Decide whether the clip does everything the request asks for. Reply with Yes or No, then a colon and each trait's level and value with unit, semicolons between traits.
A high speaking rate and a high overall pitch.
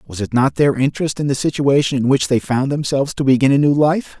No: fast, 255 wpm; low, 135 Hz